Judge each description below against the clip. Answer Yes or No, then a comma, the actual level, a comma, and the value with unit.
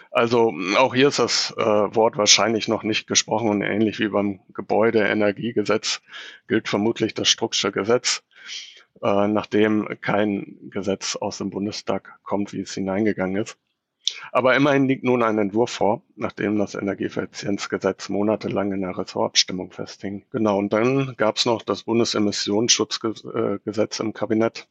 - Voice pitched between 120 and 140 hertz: No, low, 105 Hz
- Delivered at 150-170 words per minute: No, average, 140 wpm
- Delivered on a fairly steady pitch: Yes, narrow, 1.7 semitones